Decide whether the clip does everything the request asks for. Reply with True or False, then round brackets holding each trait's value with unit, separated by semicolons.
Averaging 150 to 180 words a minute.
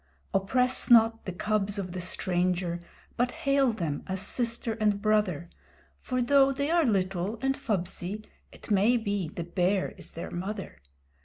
True (155 wpm)